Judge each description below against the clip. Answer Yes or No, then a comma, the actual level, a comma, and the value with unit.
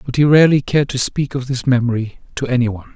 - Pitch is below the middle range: Yes, low, 130 Hz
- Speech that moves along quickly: Yes, fast, 245 wpm